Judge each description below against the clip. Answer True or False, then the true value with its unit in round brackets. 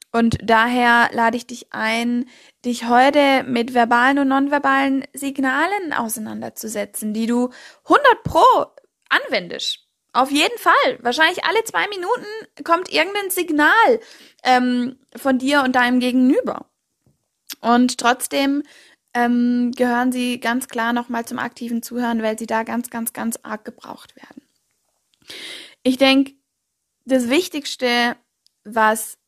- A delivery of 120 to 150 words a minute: True (125 wpm)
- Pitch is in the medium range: False (250 Hz)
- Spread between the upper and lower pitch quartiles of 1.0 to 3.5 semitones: True (2.9 semitones)